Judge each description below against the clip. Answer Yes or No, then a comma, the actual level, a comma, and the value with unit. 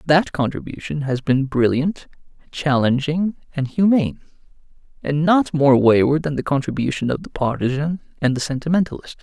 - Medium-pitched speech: Yes, medium, 145 Hz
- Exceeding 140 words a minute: No, slow, 135 wpm